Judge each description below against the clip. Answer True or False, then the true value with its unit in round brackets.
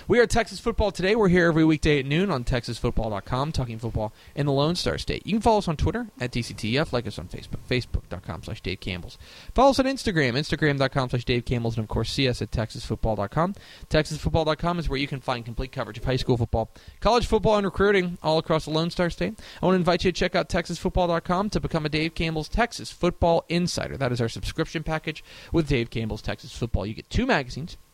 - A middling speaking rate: False (225 wpm)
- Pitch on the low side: False (150 Hz)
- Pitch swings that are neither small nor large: False (6.7 semitones)